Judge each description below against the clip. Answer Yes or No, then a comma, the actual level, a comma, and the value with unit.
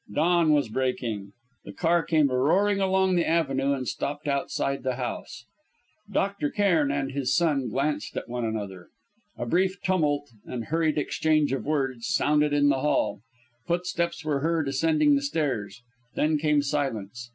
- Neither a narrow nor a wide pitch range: Yes, average, 3.9 semitones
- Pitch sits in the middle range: Yes, medium, 145 Hz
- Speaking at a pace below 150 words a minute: No, average, 155 wpm